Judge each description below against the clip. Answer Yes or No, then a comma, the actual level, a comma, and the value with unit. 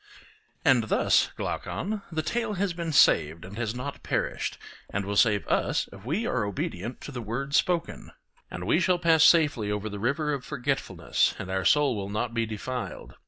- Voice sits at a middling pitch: No, low, 125 Hz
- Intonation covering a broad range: Yes, wide, 7.3 semitones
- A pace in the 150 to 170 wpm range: No, average, 185 wpm